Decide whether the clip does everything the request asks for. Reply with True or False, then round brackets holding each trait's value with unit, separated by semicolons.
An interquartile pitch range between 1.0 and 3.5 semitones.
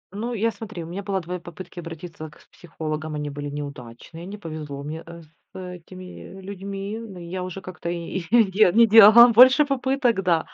False (4.2 semitones)